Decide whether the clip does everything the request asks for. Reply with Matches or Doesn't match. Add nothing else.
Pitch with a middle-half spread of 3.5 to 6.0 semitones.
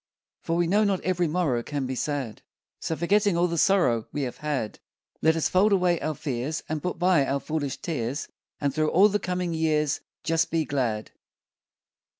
Matches